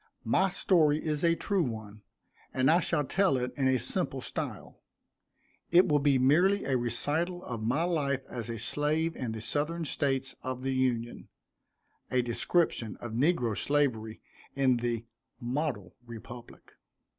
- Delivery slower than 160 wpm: Yes, average, 150 wpm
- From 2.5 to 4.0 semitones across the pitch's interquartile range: No, average, 4.7 semitones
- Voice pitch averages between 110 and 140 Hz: Yes, low, 135 Hz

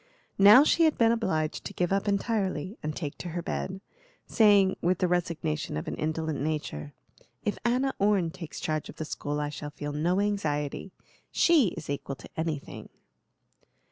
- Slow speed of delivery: No, average, 170 wpm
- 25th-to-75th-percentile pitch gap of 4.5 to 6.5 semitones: Yes, average, 5.1 semitones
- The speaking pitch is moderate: Yes, medium, 175 Hz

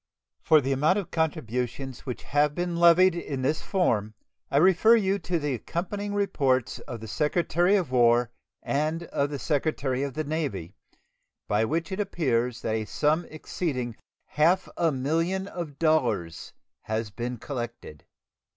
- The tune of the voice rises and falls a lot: Yes, wide, 5.7 semitones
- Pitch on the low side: No, medium, 150 Hz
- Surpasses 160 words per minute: No, average, 150 wpm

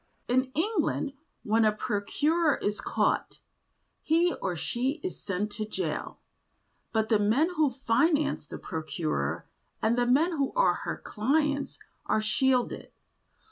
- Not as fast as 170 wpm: Yes, slow, 135 wpm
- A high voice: Yes, very high, 250 Hz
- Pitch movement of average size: No, wide, 6.0 semitones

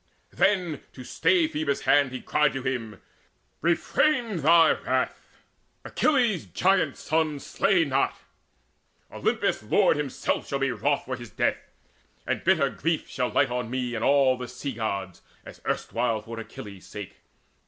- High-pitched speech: No, low, 135 Hz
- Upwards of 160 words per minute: No, average, 145 wpm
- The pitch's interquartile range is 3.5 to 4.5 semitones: No, average, 5.1 semitones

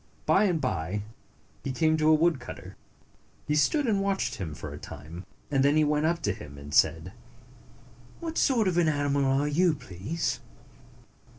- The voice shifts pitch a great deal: Yes, wide, 8.4 semitones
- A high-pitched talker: No, medium, 150 Hz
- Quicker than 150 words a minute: Yes, average, 175 wpm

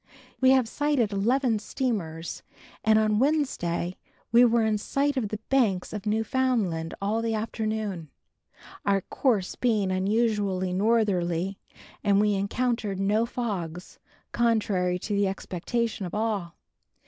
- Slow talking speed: Yes, slow, 125 wpm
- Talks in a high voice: Yes, high, 210 Hz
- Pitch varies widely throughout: No, average, 3.5 semitones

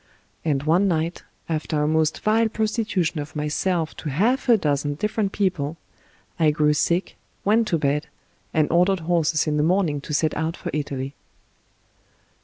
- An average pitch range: Yes, average, 4.2 semitones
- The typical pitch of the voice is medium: Yes, medium, 160 Hz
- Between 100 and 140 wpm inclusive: No, average, 160 wpm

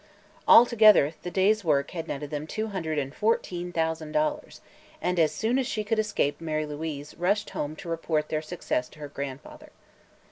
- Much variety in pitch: Yes, wide, 5.8 semitones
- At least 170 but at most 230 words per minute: Yes, average, 180 wpm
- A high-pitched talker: No, medium, 165 Hz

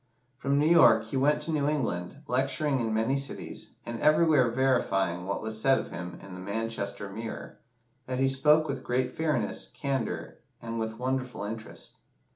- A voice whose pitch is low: Yes, low, 130 Hz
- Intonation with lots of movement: No, average, 4.0 semitones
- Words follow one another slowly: No, average, 170 wpm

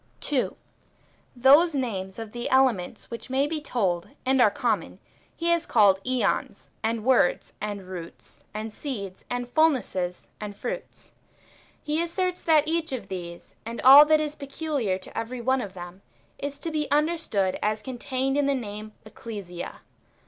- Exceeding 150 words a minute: Yes, average, 160 wpm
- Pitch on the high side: Yes, high, 245 Hz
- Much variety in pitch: Yes, wide, 6.1 semitones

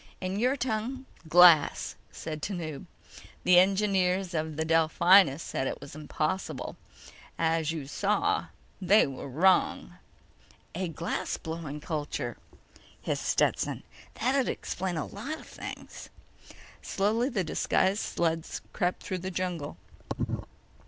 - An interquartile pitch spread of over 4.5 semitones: No, average, 3.9 semitones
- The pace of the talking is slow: Yes, slow, 110 wpm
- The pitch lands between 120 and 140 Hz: No, medium, 180 Hz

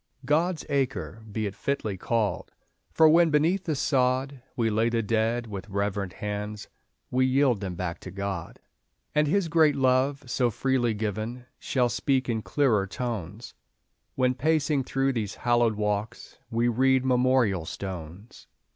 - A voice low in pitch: Yes, low, 120 Hz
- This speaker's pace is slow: No, average, 145 wpm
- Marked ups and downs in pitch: No, average, 4.4 semitones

